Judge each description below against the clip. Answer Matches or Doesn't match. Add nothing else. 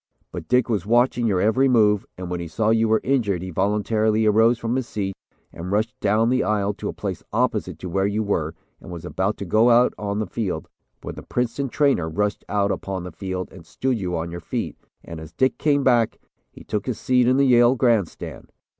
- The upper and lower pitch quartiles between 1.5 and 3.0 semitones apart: Doesn't match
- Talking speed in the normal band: Doesn't match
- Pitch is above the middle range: Doesn't match